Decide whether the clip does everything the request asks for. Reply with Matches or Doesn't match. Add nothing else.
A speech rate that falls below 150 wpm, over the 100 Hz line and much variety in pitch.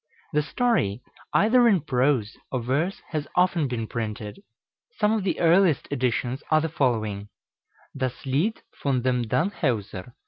Matches